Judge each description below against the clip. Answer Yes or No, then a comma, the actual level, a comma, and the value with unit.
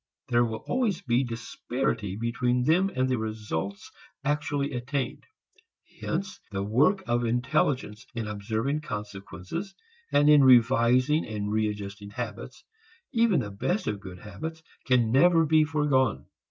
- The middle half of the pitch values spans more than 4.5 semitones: Yes, wide, 5.5 semitones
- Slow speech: Yes, slow, 130 wpm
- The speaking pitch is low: Yes, low, 125 Hz